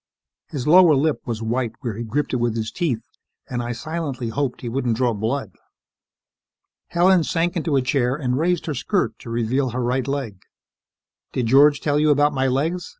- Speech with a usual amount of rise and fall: Yes, average, 4.0 semitones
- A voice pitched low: Yes, low, 130 Hz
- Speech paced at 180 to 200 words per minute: Yes, average, 190 wpm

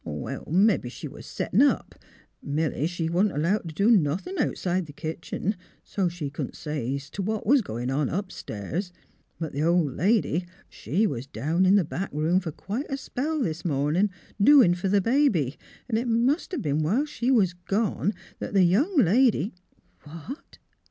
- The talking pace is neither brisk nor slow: Yes, average, 185 wpm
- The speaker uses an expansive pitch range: Yes, wide, 6.2 semitones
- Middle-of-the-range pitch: Yes, medium, 180 Hz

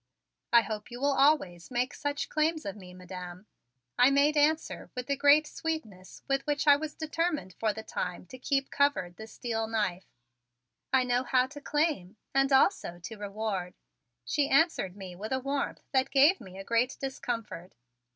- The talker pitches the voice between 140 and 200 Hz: No, very high, 250 Hz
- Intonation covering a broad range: Yes, wide, 6.4 semitones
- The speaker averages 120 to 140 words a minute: No, average, 175 wpm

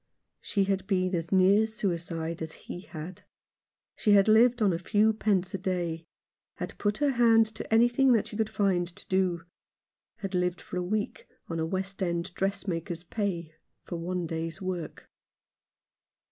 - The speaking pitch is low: No, medium, 185 Hz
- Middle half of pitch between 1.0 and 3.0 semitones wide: No, average, 3.4 semitones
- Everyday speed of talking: Yes, average, 165 wpm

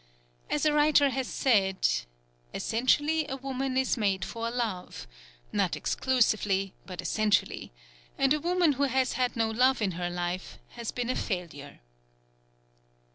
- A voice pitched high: Yes, high, 245 Hz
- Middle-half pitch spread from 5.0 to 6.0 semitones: Yes, wide, 5.6 semitones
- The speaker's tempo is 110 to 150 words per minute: Yes, average, 140 wpm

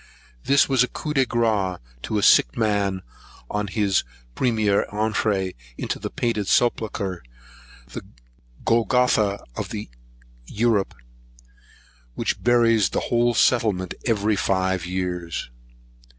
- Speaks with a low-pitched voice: Yes, low, 105 Hz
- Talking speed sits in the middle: No, slow, 110 wpm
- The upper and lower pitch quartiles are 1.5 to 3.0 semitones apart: No, average, 3.6 semitones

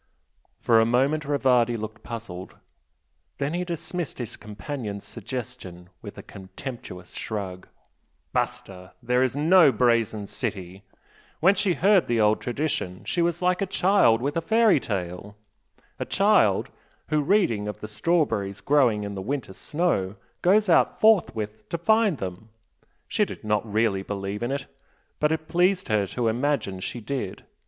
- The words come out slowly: No, average, 150 wpm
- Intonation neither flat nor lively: No, wide, 7.3 semitones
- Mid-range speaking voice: No, low, 120 Hz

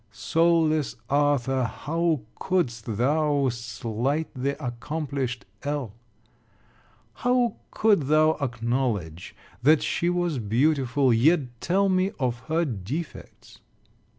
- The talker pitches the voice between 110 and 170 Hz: Yes, medium, 140 Hz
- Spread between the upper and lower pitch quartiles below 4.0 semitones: No, average, 5.0 semitones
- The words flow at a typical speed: No, slow, 100 wpm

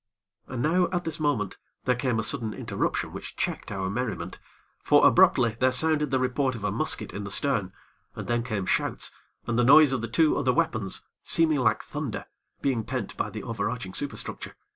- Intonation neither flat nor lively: Yes, average, 4.6 semitones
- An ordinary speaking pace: Yes, average, 195 wpm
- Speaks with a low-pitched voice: Yes, low, 125 Hz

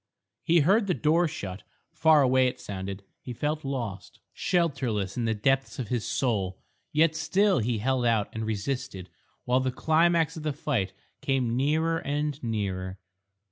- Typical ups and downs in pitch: No, wide, 6.1 semitones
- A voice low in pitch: Yes, low, 130 Hz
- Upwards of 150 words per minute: Yes, average, 160 wpm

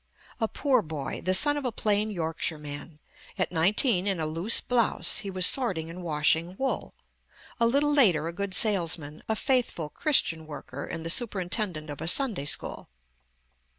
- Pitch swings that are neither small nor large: No, wide, 6.0 semitones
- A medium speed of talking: Yes, average, 170 wpm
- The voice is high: No, medium, 180 Hz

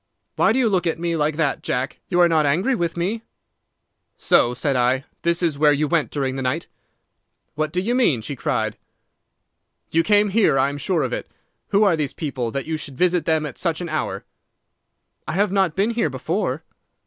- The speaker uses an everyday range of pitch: Yes, average, 4.5 semitones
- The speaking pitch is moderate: Yes, medium, 160 Hz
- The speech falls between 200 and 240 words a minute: Yes, fast, 205 wpm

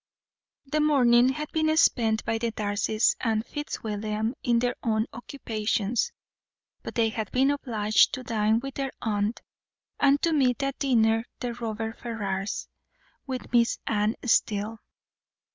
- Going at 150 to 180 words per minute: No, average, 140 wpm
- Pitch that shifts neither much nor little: Yes, average, 3.1 semitones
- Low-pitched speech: No, high, 230 Hz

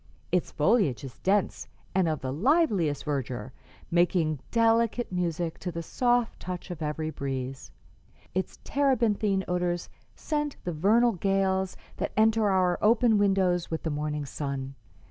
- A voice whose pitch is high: No, medium, 180 Hz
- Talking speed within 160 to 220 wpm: No, average, 140 wpm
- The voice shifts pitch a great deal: Yes, wide, 5.8 semitones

